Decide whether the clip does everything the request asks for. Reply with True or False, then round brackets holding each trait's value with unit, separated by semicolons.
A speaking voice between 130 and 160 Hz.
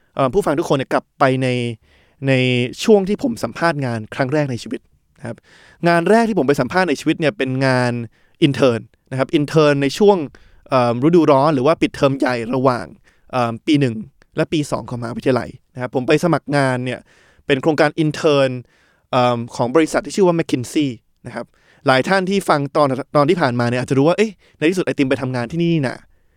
True (140 Hz)